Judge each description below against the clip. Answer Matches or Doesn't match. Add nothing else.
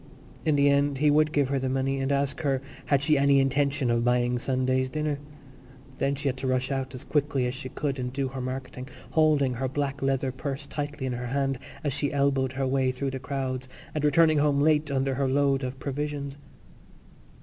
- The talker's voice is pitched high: Doesn't match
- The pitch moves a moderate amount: Doesn't match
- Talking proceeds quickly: Matches